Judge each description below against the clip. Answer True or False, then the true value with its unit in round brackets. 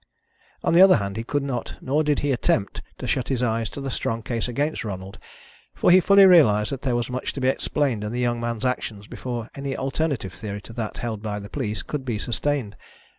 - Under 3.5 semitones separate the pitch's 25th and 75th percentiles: False (4.2 semitones)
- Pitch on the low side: True (120 Hz)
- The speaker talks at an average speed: False (230 wpm)